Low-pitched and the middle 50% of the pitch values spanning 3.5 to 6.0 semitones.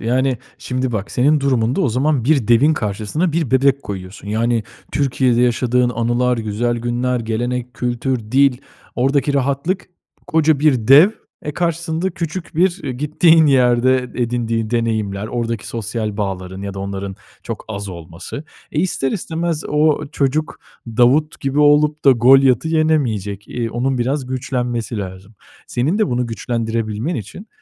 Yes: low, 125 Hz; average, 4.4 semitones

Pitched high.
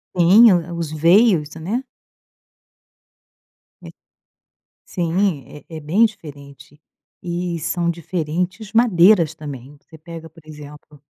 No: medium, 170 Hz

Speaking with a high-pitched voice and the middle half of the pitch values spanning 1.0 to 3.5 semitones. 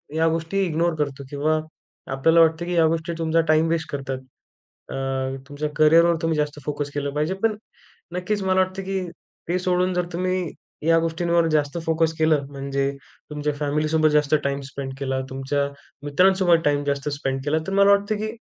No: medium, 160 Hz; average, 3.2 semitones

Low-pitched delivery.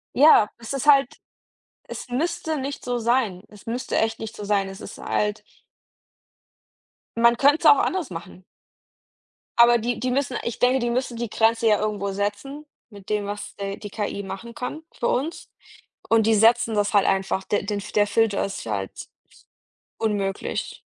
No: high, 225 Hz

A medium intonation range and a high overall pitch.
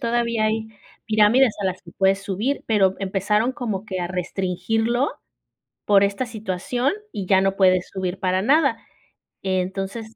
Yes: average, 3.1 semitones; high, 200 Hz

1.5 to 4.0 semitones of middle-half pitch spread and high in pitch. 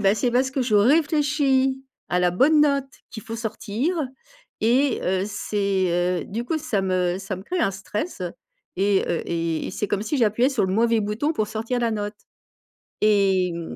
No: wide, 5.4 semitones; high, 215 Hz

